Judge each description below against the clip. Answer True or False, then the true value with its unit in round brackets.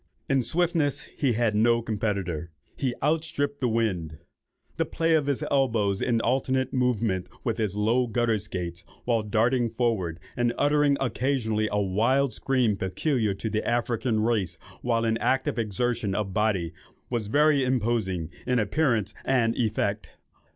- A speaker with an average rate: True (145 wpm)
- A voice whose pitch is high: False (115 Hz)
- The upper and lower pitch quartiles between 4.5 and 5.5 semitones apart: False (3.8 semitones)